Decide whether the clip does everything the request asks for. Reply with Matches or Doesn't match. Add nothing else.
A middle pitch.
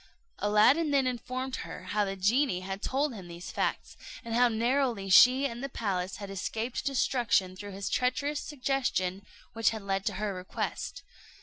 Doesn't match